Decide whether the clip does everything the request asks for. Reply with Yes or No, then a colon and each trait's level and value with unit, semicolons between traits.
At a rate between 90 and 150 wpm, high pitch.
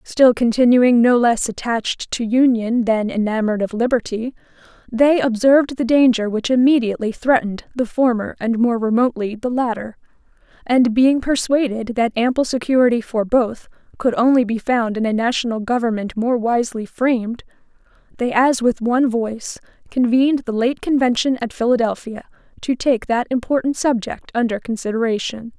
Yes: average, 145 wpm; high, 240 Hz